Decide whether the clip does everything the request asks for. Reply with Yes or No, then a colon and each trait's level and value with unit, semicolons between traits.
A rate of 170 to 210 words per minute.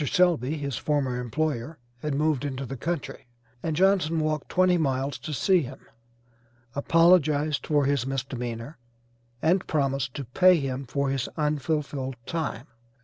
No: average, 140 wpm